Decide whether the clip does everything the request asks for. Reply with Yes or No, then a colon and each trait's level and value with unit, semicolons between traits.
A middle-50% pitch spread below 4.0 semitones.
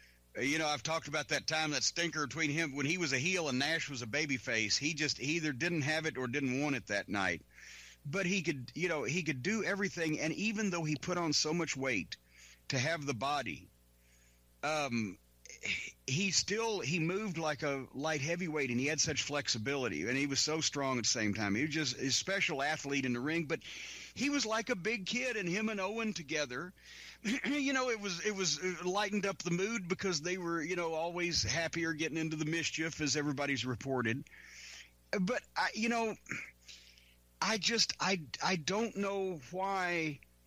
No: wide, 5.4 semitones